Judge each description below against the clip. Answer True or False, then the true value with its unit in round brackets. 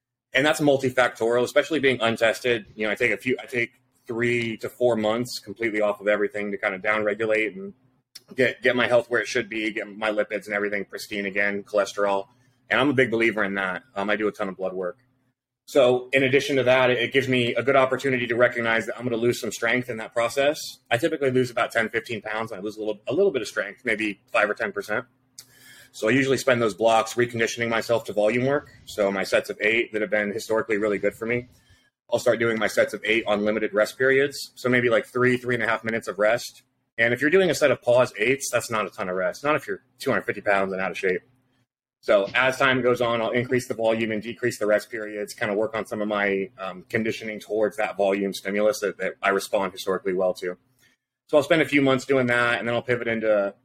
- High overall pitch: False (115 Hz)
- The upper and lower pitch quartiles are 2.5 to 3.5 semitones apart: True (3.0 semitones)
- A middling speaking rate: False (245 wpm)